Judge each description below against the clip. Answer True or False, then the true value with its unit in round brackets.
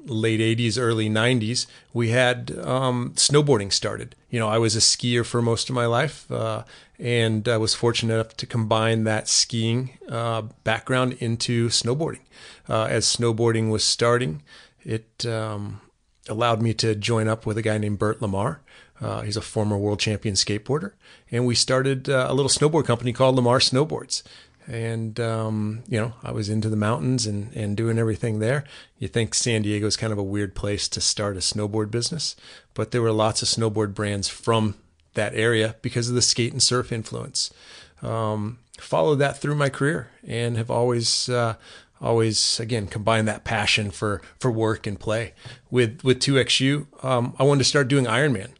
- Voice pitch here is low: True (115 Hz)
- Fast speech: False (185 wpm)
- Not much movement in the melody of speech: True (2.2 semitones)